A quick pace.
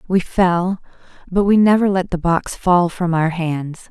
No: average, 185 wpm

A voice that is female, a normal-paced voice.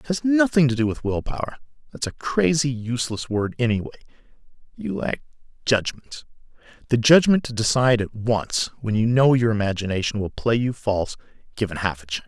No: male; average, 170 wpm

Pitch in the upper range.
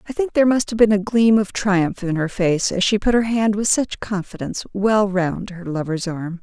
Yes: high, 200 Hz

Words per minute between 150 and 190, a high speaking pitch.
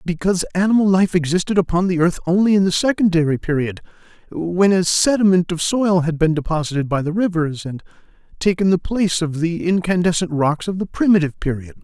No: average, 175 wpm; medium, 175 Hz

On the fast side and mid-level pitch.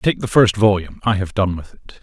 No: fast, 240 wpm; low, 100 Hz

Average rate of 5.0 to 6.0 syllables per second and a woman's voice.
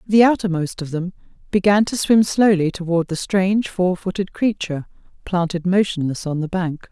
Yes: 5.1 syllables/s; female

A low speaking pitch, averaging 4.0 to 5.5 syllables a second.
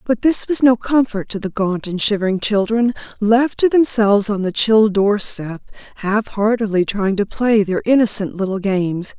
No: high, 210 Hz; 4.7 syllables/s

